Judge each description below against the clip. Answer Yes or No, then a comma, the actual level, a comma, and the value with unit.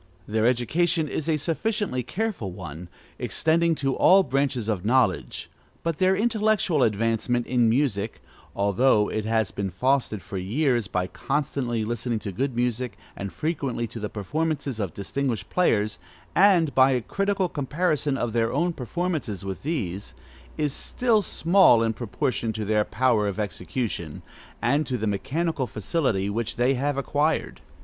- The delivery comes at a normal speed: Yes, average, 150 wpm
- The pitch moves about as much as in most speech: No, wide, 6.4 semitones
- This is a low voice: Yes, low, 125 Hz